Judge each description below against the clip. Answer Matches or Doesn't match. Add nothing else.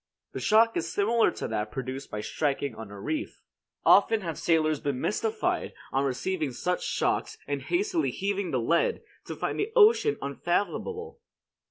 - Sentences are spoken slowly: Doesn't match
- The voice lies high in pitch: Doesn't match